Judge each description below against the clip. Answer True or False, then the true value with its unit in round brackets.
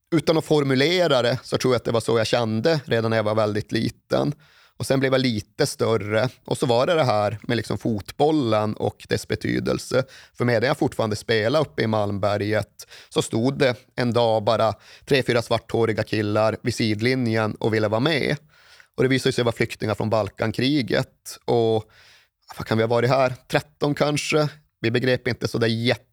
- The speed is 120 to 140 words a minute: False (190 wpm)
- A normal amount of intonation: True (3.0 semitones)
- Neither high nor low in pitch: False (115 Hz)